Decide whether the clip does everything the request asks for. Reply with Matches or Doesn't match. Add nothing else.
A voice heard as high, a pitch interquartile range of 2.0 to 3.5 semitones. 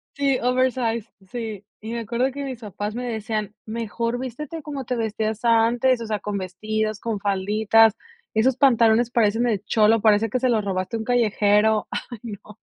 Matches